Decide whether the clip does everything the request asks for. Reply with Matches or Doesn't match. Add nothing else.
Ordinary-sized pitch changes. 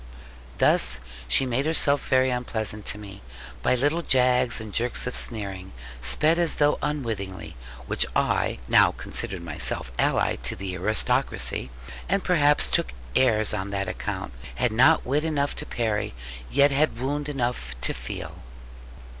Doesn't match